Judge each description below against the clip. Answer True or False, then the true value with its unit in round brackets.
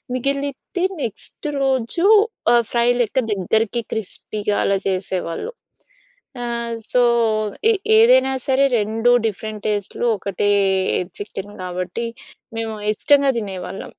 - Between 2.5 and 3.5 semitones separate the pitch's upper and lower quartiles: False (4.6 semitones)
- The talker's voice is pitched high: True (225 Hz)